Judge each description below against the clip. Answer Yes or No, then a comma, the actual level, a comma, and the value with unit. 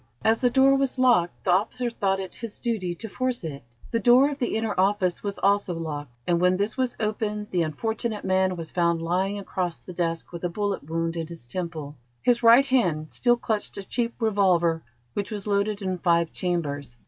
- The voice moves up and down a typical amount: Yes, average, 4.9 semitones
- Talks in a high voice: Yes, high, 195 Hz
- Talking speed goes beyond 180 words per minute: Yes, fast, 205 wpm